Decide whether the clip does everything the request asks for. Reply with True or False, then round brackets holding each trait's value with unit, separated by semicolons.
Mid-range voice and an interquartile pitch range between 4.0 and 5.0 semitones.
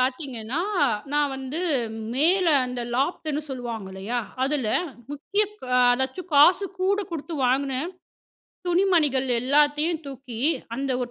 False (280 Hz; 4.3 semitones)